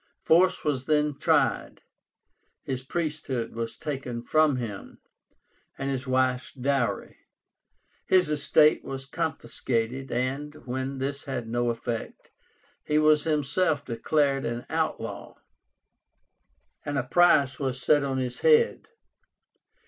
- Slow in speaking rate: Yes, slow, 115 wpm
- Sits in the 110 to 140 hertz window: Yes, low, 135 Hz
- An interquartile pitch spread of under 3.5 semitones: Yes, average, 3.0 semitones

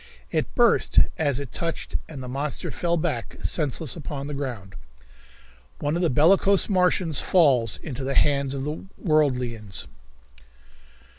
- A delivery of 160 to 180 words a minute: No, average, 140 wpm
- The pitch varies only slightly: No, average, 4.0 semitones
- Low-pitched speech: No, medium, 145 Hz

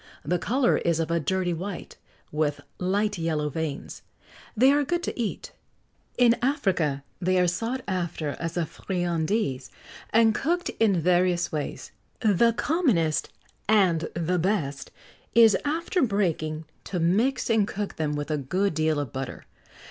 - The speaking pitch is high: No, medium, 180 Hz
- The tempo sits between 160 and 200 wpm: No, average, 150 wpm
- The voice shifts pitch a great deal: Yes, wide, 5.7 semitones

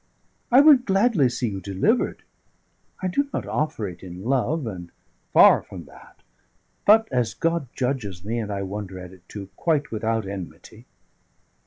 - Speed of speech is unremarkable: Yes, average, 160 wpm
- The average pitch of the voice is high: No, low, 115 Hz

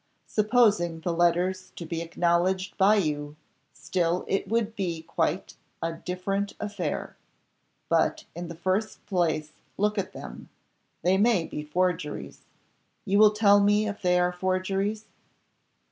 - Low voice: No, medium, 185 Hz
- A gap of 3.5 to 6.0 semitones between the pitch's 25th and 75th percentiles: No, average, 3.1 semitones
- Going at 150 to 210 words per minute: No, slow, 135 wpm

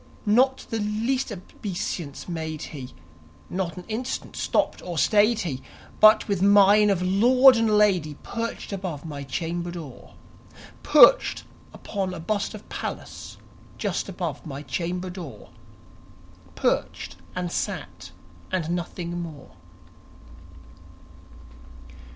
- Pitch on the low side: No, medium, 180 Hz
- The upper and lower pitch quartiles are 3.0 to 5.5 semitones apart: Yes, average, 4.1 semitones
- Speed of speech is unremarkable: No, slow, 115 wpm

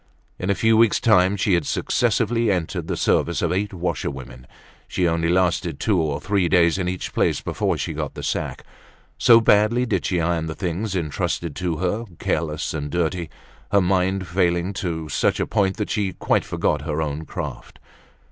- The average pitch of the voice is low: Yes, very low, 90 Hz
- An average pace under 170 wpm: No, average, 185 wpm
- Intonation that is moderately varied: Yes, average, 3.4 semitones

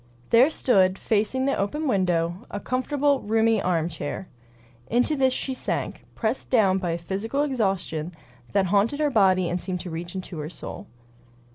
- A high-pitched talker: Yes, high, 200 Hz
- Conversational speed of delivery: Yes, average, 160 wpm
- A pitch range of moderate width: No, wide, 6.0 semitones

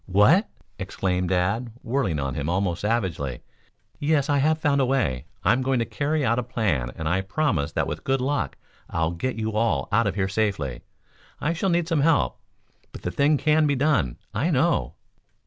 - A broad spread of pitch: Yes, wide, 8.1 semitones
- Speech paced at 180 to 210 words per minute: Yes, average, 190 wpm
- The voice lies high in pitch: No, low, 115 Hz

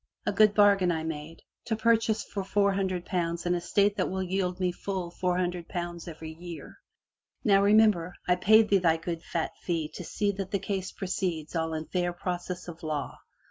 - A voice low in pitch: No, medium, 180 Hz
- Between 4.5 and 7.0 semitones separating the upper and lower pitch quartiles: No, average, 2.7 semitones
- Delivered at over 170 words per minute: Yes, average, 200 wpm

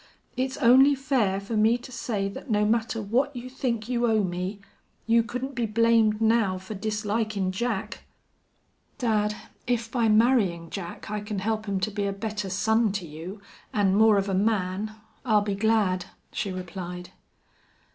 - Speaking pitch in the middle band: No, high, 215 Hz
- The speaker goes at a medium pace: Yes, average, 165 wpm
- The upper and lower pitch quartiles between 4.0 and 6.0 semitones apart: No, average, 2.9 semitones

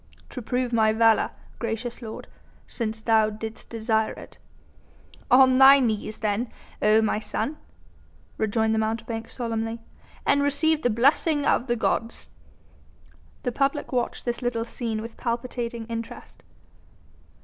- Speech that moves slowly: Yes, slow, 130 wpm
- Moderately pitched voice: No, high, 230 Hz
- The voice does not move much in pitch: Yes, narrow, 2.1 semitones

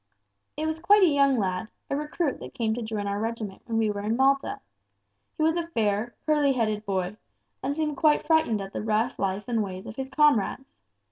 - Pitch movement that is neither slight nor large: No, wide, 6.1 semitones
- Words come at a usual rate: No, fast, 210 wpm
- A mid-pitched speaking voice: No, high, 235 Hz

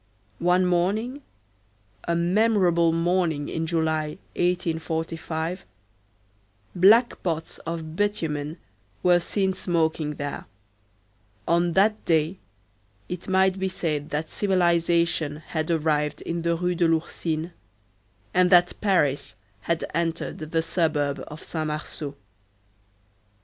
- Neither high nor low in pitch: Yes, medium, 165 Hz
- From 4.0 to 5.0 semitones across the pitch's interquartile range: No, average, 2.8 semitones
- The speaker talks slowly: Yes, slow, 100 wpm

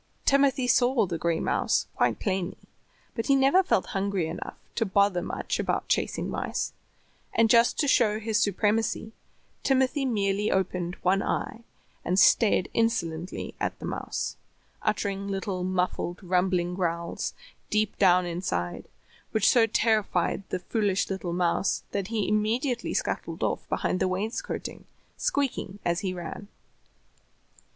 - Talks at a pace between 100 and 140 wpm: Yes, slow, 135 wpm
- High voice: Yes, high, 200 Hz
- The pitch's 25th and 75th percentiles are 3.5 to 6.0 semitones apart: Yes, average, 3.8 semitones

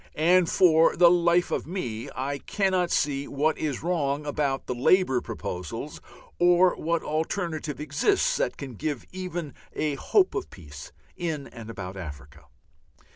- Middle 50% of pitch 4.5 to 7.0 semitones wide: Yes, average, 4.8 semitones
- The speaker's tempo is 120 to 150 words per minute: Yes, average, 145 wpm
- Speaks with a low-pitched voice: No, medium, 155 Hz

